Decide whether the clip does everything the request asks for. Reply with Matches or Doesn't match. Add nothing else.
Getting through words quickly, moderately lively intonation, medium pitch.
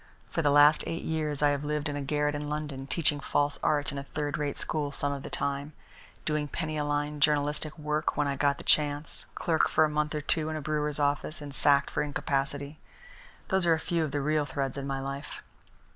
Doesn't match